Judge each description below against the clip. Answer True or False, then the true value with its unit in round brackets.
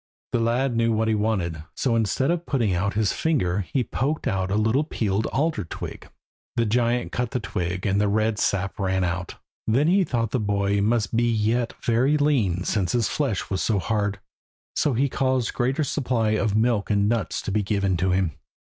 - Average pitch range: True (3.7 semitones)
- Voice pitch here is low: True (110 Hz)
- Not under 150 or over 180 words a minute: False (200 wpm)